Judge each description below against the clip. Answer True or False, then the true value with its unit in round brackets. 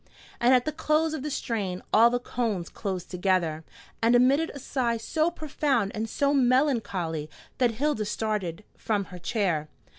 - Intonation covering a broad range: True (6.1 semitones)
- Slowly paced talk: False (160 wpm)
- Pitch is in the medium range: False (230 Hz)